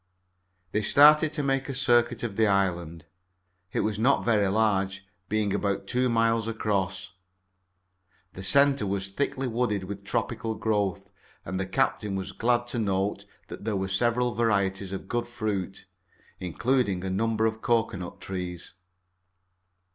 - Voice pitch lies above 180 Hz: No, low, 105 Hz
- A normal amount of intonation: Yes, average, 3.7 semitones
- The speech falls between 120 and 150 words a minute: Yes, average, 145 wpm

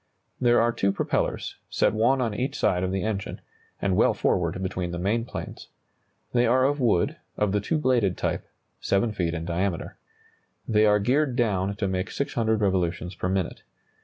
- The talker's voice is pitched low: Yes, low, 100 Hz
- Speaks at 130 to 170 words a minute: No, average, 180 wpm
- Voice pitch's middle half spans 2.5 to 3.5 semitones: No, average, 4.3 semitones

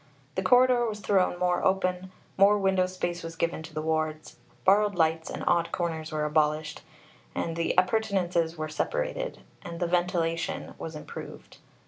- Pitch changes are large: No, average, 3.0 semitones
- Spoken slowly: No, average, 150 wpm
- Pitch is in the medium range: Yes, medium, 175 Hz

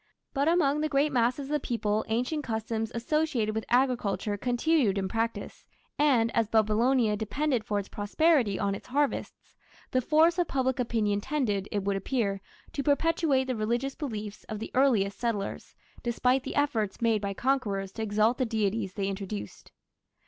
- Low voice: No, high, 230 Hz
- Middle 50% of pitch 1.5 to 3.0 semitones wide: No, average, 4.7 semitones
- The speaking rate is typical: Yes, average, 165 wpm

